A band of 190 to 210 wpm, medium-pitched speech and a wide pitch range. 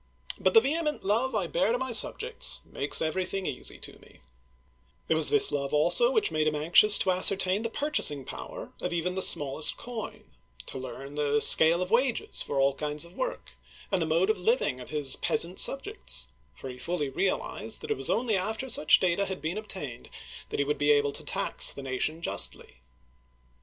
Yes: average, 200 wpm; medium, 180 Hz; wide, 7.0 semitones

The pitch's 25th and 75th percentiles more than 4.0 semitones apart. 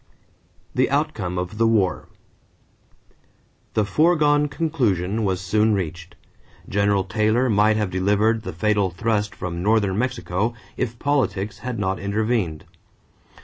No: average, 3.5 semitones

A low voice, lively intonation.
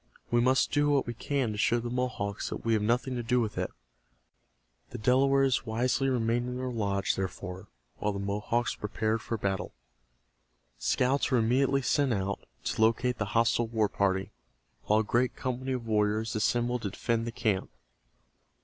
No: low, 115 Hz; average, 2.9 semitones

